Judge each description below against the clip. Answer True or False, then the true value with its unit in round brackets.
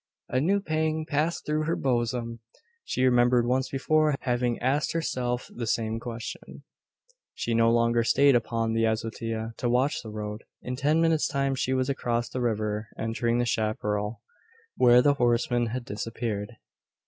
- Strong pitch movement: False (3.0 semitones)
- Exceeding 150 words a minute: True (160 wpm)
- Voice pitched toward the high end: False (120 Hz)